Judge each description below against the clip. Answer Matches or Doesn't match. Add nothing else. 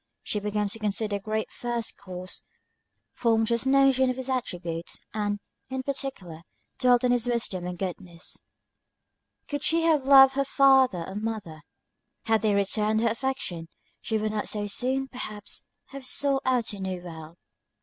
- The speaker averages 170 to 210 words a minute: Doesn't match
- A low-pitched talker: Doesn't match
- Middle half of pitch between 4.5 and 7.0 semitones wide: Matches